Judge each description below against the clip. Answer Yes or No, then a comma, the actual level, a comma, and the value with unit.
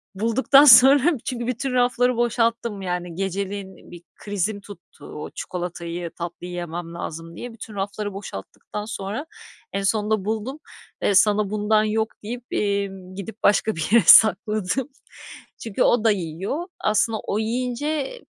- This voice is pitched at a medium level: No, high, 210 Hz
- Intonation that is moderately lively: Yes, average, 3.7 semitones